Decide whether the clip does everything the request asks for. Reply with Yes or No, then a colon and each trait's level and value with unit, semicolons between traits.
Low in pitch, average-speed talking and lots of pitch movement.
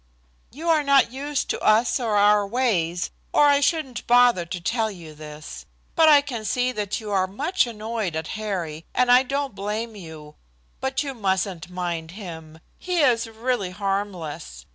No: high, 215 Hz; average, 170 wpm; wide, 6.0 semitones